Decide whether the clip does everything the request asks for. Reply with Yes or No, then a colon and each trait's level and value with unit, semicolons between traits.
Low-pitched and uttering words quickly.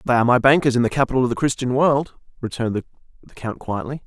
Yes: low, 125 Hz; fast, 220 wpm